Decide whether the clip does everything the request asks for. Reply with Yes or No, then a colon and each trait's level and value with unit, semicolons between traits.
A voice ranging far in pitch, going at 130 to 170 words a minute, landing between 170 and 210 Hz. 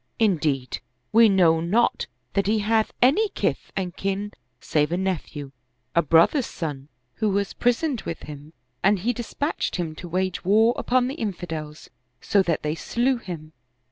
Yes: wide, 5.7 semitones; average, 165 wpm; high, 190 Hz